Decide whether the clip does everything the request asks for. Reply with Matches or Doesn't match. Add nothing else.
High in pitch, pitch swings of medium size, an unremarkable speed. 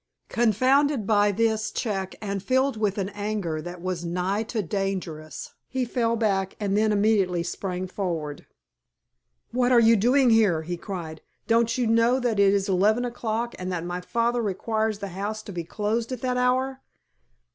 Matches